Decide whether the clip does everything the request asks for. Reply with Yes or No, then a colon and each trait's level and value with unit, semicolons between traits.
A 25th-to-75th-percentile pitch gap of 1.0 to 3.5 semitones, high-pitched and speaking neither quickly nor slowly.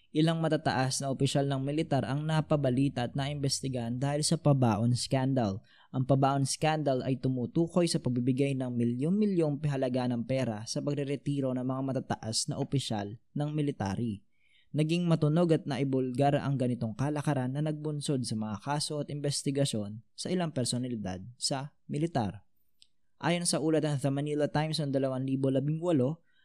No: average, 2.9 semitones; medium, 140 Hz; average, 145 wpm